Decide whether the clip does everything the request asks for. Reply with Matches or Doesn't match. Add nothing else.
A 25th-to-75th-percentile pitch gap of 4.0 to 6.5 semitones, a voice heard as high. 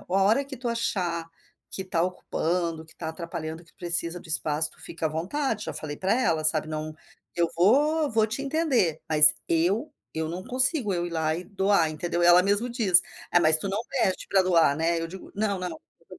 Doesn't match